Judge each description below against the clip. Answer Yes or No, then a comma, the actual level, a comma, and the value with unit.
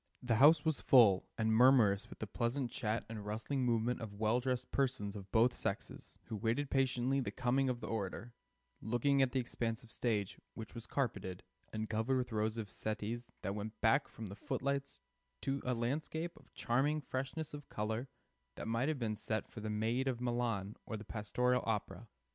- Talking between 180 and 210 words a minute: Yes, average, 190 wpm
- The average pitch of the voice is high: No, low, 120 Hz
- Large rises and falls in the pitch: No, average, 3.3 semitones